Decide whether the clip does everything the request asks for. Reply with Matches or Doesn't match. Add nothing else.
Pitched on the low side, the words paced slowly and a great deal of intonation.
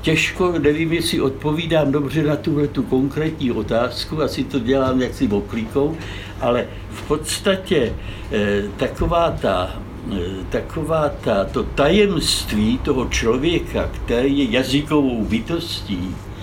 Matches